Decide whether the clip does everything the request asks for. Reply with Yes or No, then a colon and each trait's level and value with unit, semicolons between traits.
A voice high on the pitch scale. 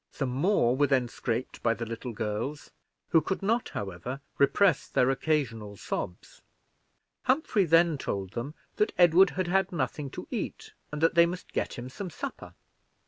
No: medium, 145 Hz